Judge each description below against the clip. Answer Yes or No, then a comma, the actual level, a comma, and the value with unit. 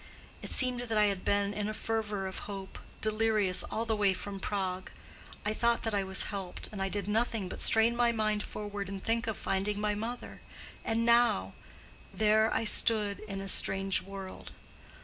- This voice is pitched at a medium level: No, high, 210 Hz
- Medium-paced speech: Yes, average, 175 wpm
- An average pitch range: No, narrow, 2.3 semitones